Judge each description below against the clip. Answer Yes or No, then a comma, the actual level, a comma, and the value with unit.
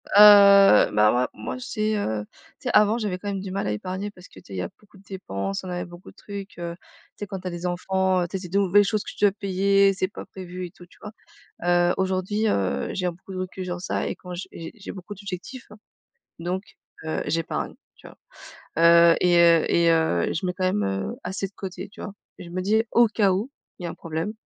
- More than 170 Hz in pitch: Yes, medium, 185 Hz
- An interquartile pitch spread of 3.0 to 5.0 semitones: No, narrow, 2.6 semitones